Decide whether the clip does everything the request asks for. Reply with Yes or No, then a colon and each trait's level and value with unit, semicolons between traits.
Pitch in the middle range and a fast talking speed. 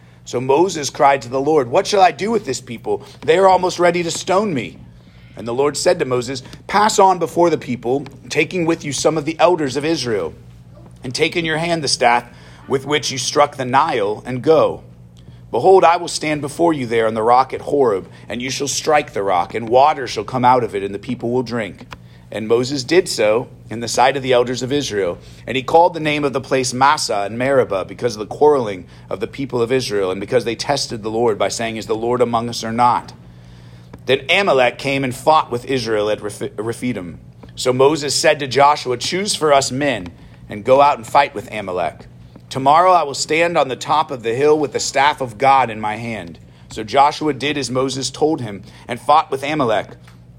No: low, 130 Hz; fast, 220 wpm